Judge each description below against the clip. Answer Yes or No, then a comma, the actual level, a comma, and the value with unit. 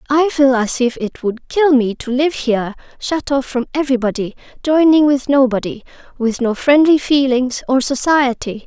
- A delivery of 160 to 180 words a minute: No, average, 150 wpm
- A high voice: Yes, very high, 265 Hz